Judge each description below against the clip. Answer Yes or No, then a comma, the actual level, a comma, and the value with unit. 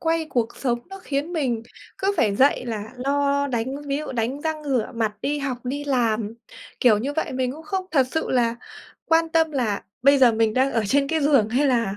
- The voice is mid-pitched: No, very high, 270 Hz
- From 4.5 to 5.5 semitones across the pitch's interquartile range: No, average, 4.0 semitones